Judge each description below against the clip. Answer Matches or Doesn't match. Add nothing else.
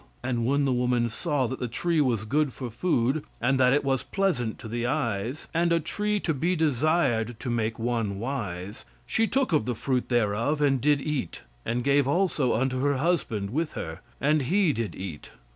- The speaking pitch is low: Matches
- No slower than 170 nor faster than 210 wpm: Matches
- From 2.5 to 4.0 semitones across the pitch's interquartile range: Doesn't match